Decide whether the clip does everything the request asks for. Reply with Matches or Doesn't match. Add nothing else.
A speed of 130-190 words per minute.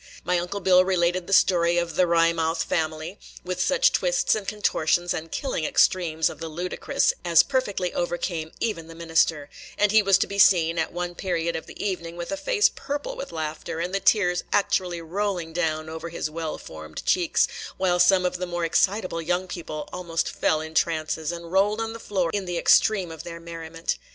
Doesn't match